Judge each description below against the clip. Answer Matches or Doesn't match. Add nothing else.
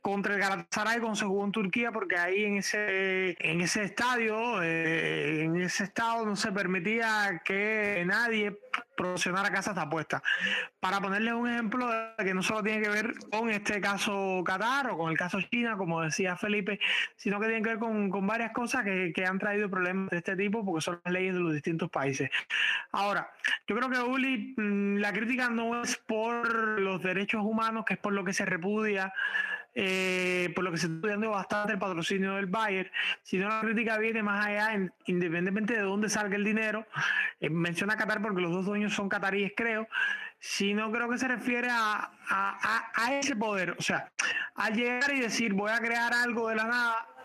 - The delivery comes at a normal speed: Doesn't match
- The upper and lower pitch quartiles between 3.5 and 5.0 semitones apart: Doesn't match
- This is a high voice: Matches